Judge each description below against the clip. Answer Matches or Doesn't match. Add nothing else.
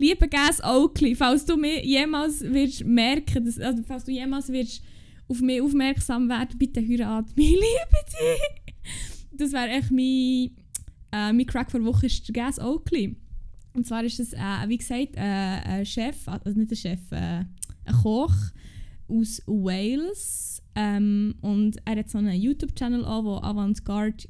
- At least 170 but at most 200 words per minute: Doesn't match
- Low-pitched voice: Doesn't match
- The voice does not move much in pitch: Doesn't match